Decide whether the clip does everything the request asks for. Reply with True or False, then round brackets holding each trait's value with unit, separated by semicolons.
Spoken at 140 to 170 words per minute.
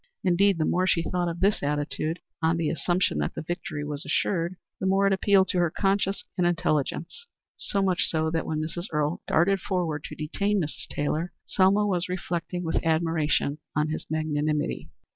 False (180 wpm)